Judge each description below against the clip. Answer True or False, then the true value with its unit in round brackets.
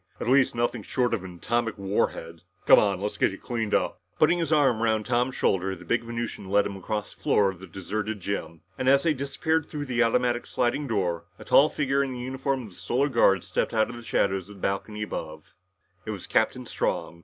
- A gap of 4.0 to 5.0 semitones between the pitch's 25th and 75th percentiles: True (4.6 semitones)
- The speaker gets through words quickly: True (230 wpm)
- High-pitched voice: False (115 Hz)